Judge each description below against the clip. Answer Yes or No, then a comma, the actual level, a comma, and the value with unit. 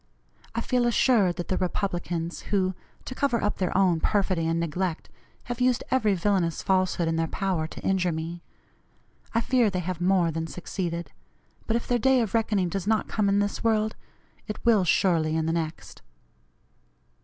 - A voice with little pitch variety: No, average, 4.2 semitones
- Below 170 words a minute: No, average, 180 wpm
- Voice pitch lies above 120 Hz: Yes, high, 190 Hz